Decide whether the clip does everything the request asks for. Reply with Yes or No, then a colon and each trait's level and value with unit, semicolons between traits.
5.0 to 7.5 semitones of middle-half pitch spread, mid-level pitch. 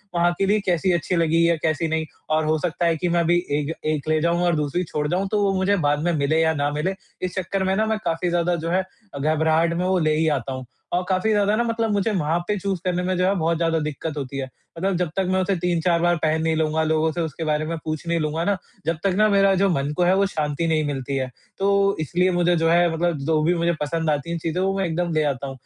No: average, 2.8 semitones; medium, 170 Hz